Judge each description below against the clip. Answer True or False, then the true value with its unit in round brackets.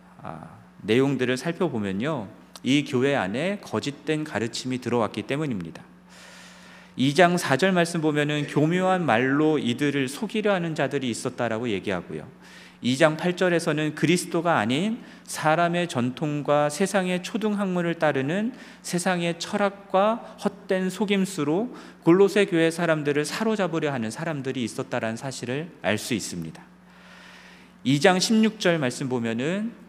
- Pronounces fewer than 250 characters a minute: False (295 characters per minute)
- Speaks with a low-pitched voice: False (160 Hz)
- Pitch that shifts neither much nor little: False (5.7 semitones)